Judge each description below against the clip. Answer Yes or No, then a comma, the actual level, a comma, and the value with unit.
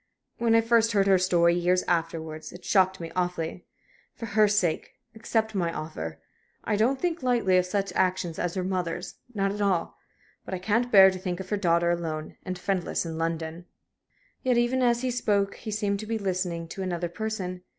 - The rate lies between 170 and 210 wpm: Yes, average, 195 wpm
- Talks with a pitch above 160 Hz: Yes, medium, 185 Hz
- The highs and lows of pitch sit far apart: No, average, 3.7 semitones